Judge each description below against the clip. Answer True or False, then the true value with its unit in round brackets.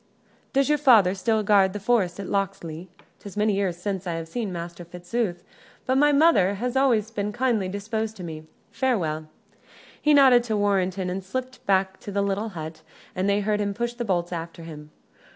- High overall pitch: True (200 Hz)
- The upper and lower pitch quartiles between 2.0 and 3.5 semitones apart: False (4.1 semitones)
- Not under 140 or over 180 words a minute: False (190 wpm)